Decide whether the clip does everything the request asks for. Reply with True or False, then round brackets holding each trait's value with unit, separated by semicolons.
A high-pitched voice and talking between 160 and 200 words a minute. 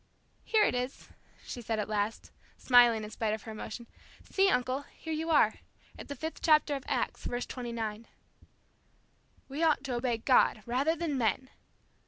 True (250 Hz; 170 wpm)